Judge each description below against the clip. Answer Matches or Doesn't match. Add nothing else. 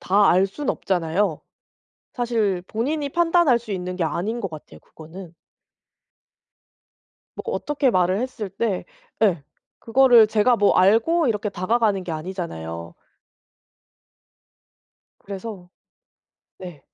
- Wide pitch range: Doesn't match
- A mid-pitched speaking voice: Doesn't match